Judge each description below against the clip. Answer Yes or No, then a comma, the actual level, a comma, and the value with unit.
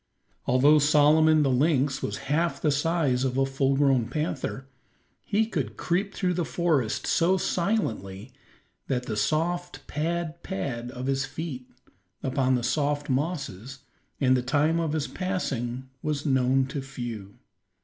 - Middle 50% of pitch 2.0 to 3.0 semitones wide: No, average, 4.0 semitones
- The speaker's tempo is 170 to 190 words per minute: No, average, 145 wpm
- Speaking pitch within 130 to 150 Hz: Yes, medium, 140 Hz